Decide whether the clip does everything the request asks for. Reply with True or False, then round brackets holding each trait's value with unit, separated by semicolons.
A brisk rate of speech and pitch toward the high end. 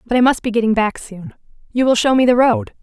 True (275 wpm; 240 Hz)